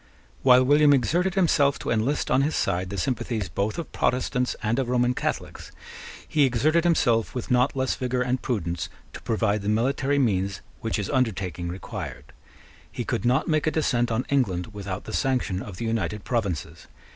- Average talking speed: Yes, average, 180 wpm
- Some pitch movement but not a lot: Yes, average, 4.7 semitones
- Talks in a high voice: No, low, 120 Hz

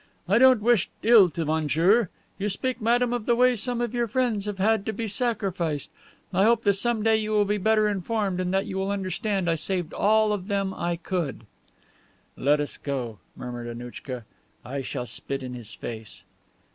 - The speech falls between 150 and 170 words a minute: No, average, 195 wpm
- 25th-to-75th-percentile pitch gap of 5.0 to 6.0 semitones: Yes, wide, 5.6 semitones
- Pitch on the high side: Yes, high, 195 Hz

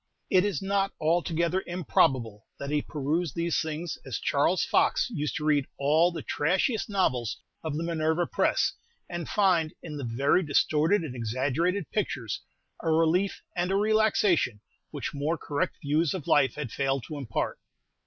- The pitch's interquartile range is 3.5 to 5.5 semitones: Yes, average, 3.9 semitones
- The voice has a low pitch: No, medium, 160 Hz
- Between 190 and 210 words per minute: No, average, 160 wpm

